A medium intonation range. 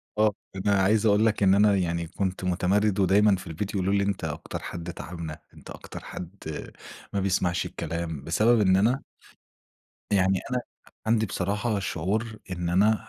Yes: average, 3.0 semitones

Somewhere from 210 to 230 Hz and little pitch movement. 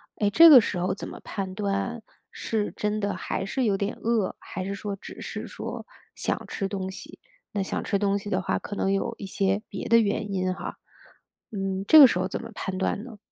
No: high, 200 Hz; narrow, 1.8 semitones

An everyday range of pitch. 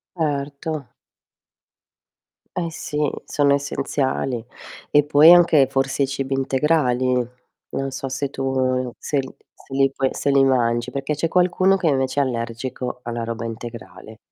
No: narrow, 2.3 semitones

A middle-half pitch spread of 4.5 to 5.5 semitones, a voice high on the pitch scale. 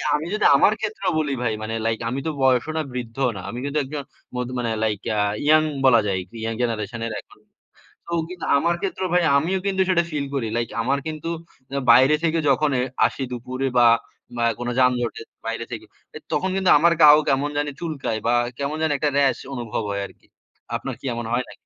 No: average, 4.8 semitones; low, 135 Hz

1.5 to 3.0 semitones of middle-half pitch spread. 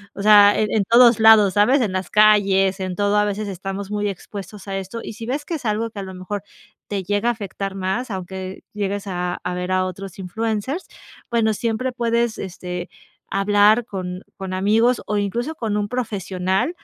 Yes: narrow, 2.6 semitones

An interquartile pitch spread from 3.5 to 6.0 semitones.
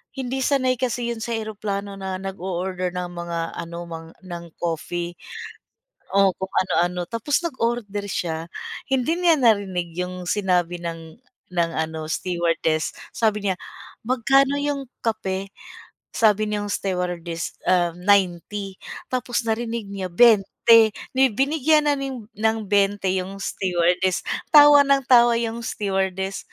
Yes: average, 4.8 semitones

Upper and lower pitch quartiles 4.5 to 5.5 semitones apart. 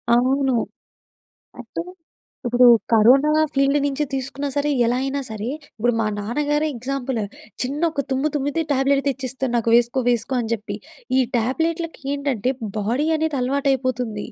No: average, 2.8 semitones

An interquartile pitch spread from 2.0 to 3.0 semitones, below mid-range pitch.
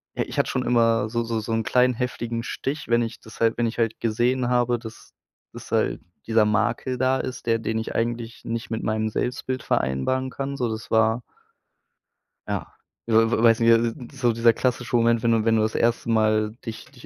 No: narrow, 1.5 semitones; low, 115 Hz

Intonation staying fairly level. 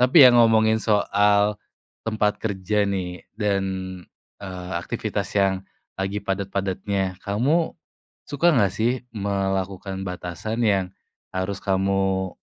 Yes: narrow, 2.3 semitones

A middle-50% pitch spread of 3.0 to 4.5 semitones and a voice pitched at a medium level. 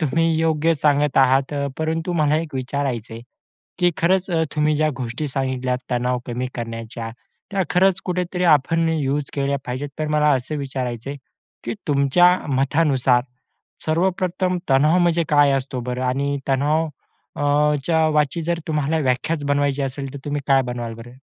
Yes: average, 3.6 semitones; medium, 145 Hz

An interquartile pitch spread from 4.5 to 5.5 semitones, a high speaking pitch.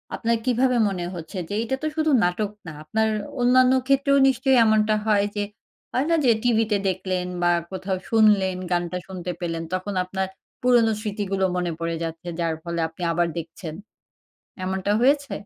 Yes: average, 5.0 semitones; high, 200 Hz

